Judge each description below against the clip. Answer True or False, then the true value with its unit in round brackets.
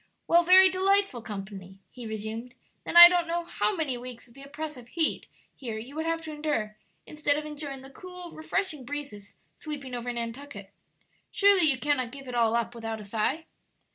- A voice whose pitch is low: False (275 Hz)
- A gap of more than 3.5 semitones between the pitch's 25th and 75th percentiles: True (5.6 semitones)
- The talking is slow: False (185 wpm)